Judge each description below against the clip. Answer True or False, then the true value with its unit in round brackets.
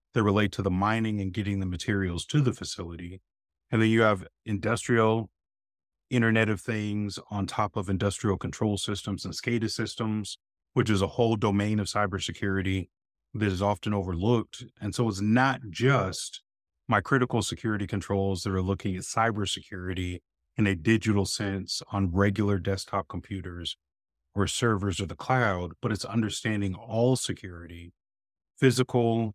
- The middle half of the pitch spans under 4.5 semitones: True (2.9 semitones)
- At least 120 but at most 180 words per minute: True (150 wpm)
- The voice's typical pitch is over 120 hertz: False (100 Hz)